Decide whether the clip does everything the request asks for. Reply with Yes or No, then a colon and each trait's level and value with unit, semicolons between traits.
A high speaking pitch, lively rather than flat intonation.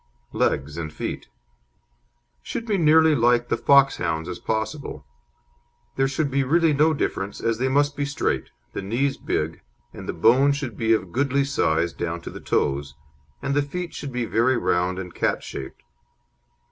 No: low, 125 Hz; wide, 7.8 semitones